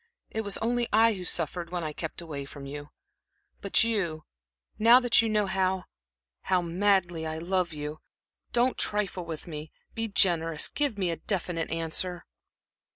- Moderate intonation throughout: Yes, average, 4.3 semitones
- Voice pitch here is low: No, medium, 180 Hz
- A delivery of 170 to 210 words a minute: No, average, 160 wpm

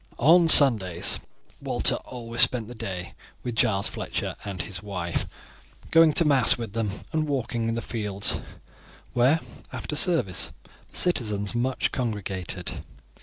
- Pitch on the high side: No, low, 115 Hz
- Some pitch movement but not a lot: Yes, average, 4.7 semitones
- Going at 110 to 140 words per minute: Yes, slow, 135 wpm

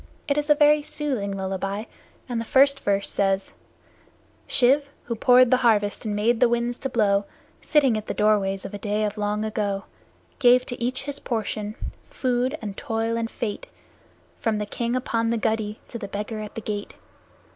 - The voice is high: Yes, high, 225 Hz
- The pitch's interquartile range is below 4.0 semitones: Yes, average, 3.3 semitones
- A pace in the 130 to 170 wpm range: No, average, 185 wpm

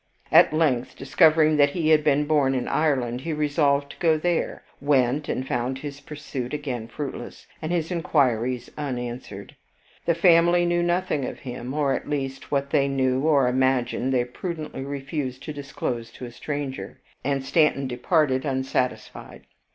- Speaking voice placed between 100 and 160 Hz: Yes, medium, 140 Hz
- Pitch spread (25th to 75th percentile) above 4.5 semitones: No, average, 3.0 semitones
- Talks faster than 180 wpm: No, average, 160 wpm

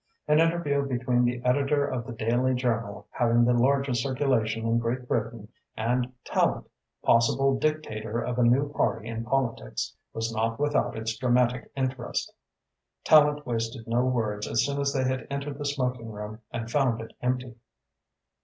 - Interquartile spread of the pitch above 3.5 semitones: No, average, 3.0 semitones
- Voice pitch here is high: No, low, 125 Hz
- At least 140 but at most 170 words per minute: Yes, average, 160 wpm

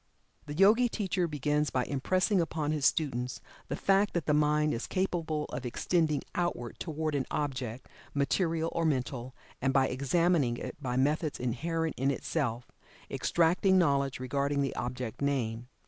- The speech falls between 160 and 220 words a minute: No, average, 150 wpm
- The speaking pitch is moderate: Yes, medium, 145 Hz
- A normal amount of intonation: Yes, average, 4.2 semitones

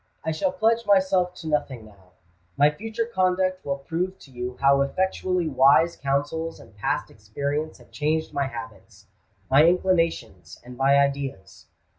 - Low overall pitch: No, medium, 150 Hz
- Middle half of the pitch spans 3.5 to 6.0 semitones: Yes, average, 5.3 semitones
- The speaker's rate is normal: Yes, average, 150 wpm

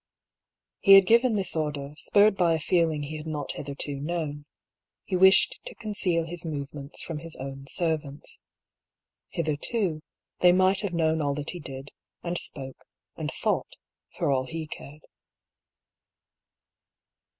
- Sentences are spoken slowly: No, average, 145 wpm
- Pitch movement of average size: Yes, average, 3.7 semitones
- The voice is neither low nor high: Yes, medium, 160 Hz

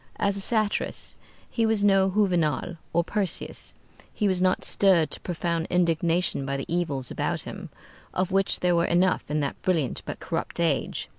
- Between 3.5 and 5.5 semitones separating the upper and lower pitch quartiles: No, average, 2.8 semitones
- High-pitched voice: No, medium, 180 Hz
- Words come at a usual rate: Yes, average, 170 wpm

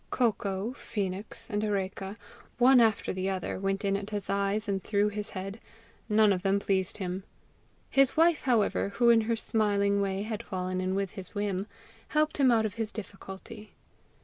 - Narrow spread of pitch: Yes, narrow, 2.2 semitones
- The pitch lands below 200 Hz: No, high, 205 Hz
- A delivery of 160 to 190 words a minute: Yes, average, 175 wpm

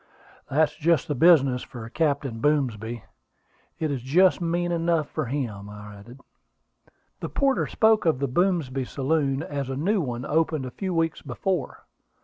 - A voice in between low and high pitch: Yes, medium, 145 Hz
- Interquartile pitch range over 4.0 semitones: Yes, average, 4.6 semitones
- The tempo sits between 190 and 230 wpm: No, average, 155 wpm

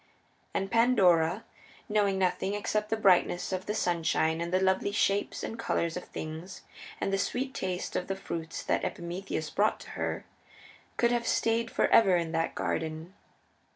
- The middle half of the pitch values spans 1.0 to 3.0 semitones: No, average, 3.7 semitones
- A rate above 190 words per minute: No, average, 160 wpm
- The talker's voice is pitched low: No, high, 190 Hz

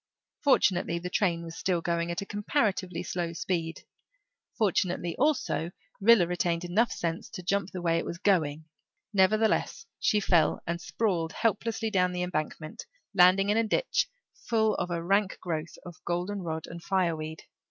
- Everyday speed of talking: Yes, average, 160 wpm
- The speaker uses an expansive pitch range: No, average, 3.3 semitones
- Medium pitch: Yes, medium, 180 Hz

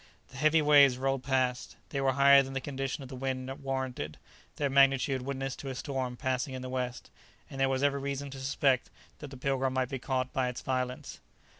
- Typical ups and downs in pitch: No, narrow, 1.2 semitones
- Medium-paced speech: No, fast, 210 wpm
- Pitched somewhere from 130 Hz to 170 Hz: Yes, low, 135 Hz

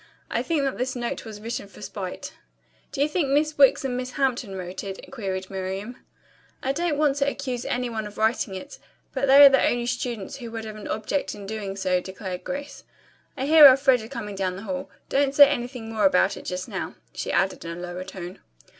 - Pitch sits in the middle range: No, high, 235 Hz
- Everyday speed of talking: No, fast, 215 wpm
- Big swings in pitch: Yes, wide, 5.8 semitones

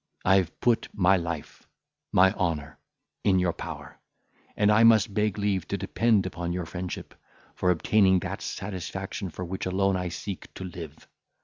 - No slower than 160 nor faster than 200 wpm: Yes, average, 165 wpm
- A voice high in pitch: No, very low, 95 Hz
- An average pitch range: No, narrow, 2.2 semitones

